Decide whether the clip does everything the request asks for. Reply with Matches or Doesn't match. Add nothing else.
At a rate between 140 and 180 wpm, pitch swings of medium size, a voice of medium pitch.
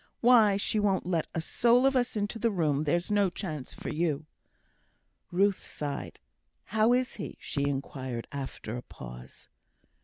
Doesn't match